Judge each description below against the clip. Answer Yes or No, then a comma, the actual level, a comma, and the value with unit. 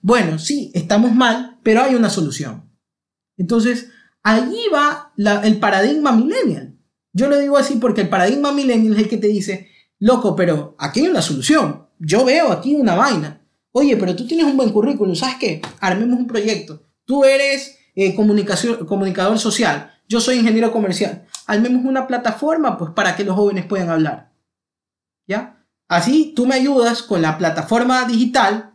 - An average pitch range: Yes, average, 4.6 semitones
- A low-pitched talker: No, high, 225 Hz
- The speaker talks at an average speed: Yes, average, 165 wpm